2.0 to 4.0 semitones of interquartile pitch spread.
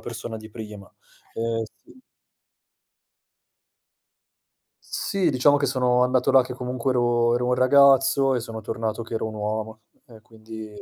Yes: narrow, 2.6 semitones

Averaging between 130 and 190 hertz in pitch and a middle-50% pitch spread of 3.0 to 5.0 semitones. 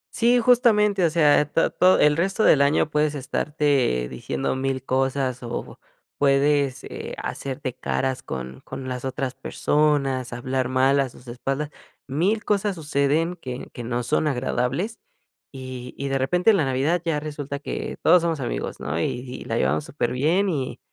Yes: medium, 140 Hz; average, 3.6 semitones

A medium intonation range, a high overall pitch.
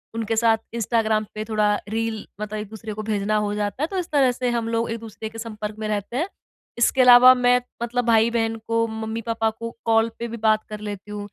No: narrow, 1.5 semitones; high, 225 Hz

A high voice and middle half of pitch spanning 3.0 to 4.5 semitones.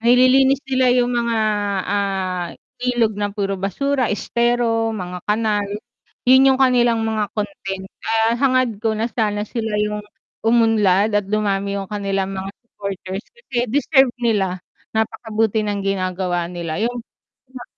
Yes: high, 220 Hz; average, 3.5 semitones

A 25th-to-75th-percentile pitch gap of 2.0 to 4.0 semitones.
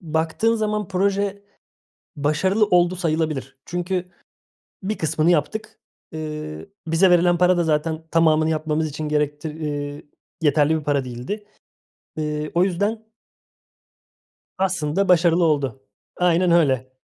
Yes: average, 3.3 semitones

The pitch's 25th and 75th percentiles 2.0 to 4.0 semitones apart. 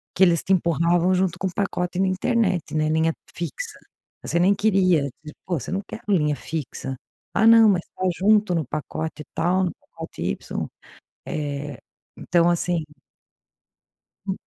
Yes: average, 3.2 semitones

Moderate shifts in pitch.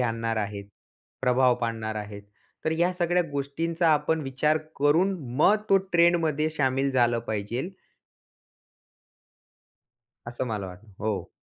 No: wide, 6.2 semitones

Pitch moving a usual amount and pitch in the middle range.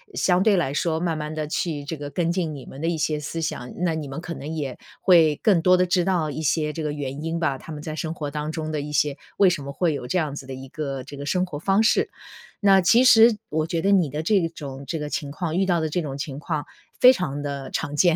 Yes: average, 3.2 semitones; medium, 155 Hz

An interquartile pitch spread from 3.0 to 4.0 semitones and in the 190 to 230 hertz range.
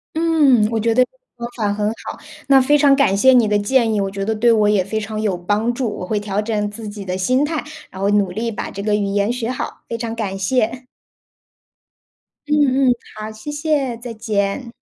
Yes: average, 3.7 semitones; high, 220 Hz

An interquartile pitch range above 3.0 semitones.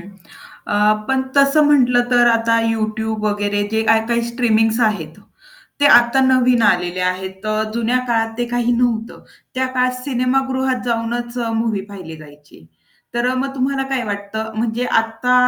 No: average, 2.7 semitones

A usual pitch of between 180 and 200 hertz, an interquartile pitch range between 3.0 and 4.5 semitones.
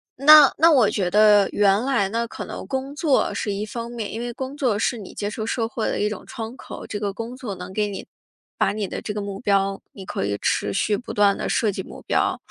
No: high, 215 Hz; average, 3.3 semitones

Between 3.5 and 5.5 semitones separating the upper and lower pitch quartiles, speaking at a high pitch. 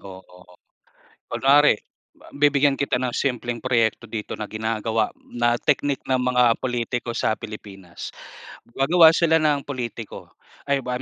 No: average, 4.0 semitones; low, 125 Hz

